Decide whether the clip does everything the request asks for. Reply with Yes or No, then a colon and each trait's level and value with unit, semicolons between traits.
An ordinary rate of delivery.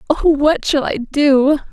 Yes: average, 175 wpm